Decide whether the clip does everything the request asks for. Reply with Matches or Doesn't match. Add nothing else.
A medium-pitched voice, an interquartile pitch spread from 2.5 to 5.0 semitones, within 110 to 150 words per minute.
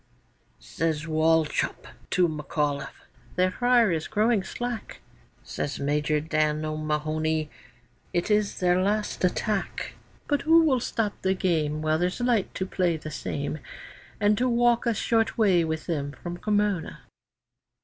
Doesn't match